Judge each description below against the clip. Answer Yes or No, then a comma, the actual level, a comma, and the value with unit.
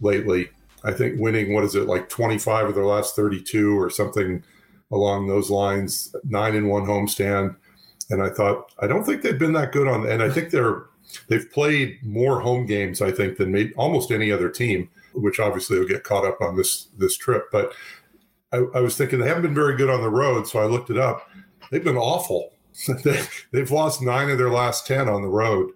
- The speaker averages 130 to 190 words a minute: No, fast, 205 wpm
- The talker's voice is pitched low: Yes, low, 115 Hz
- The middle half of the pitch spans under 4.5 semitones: No, wide, 5.5 semitones